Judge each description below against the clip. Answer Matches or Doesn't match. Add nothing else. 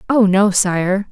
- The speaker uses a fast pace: Doesn't match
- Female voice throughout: Matches